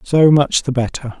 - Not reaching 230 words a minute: Yes, average, 200 wpm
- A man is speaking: Yes, male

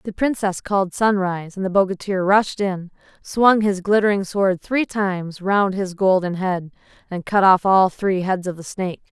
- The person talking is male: No, female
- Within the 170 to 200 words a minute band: Yes, average, 185 wpm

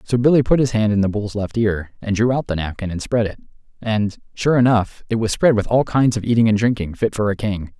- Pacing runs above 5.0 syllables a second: Yes, 5.8 syllables/s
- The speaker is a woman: No, male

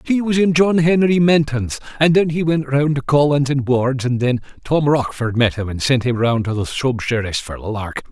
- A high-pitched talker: No, low, 135 Hz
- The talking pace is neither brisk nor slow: No, fast, 230 wpm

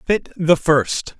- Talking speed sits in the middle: Yes, average, 150 wpm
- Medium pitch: Yes, medium, 160 Hz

